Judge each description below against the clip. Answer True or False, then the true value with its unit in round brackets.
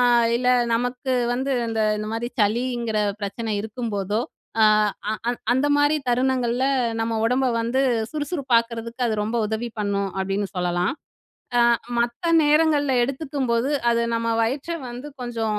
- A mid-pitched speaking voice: False (235 Hz)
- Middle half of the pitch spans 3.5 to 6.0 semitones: False (2.8 semitones)